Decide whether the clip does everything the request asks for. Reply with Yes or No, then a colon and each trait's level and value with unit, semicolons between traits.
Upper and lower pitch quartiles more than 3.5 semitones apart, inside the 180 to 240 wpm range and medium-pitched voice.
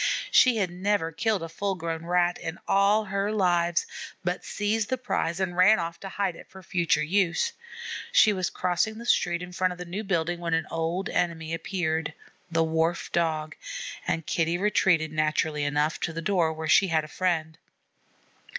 No: average, 3.1 semitones; average, 185 wpm; medium, 175 Hz